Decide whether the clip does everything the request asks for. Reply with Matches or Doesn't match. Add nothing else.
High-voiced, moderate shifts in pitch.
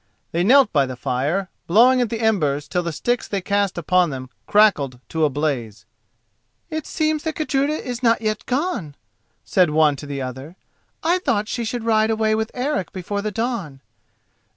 Doesn't match